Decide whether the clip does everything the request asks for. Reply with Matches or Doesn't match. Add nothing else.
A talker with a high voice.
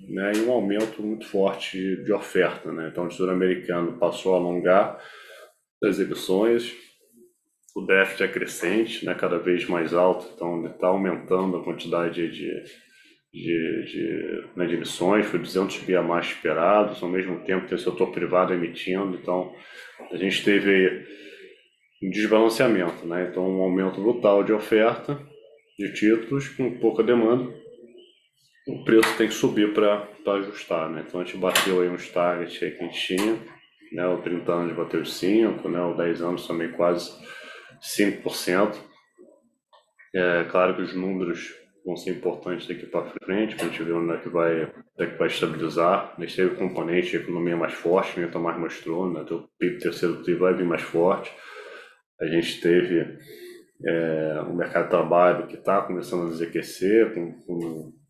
Doesn't match